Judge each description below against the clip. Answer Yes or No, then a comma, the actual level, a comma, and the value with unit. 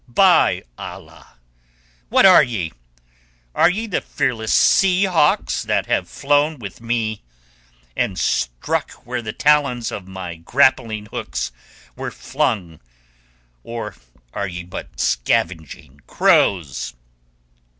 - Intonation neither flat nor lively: No, wide, 8.3 semitones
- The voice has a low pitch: Yes, low, 110 Hz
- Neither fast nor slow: No, slow, 110 wpm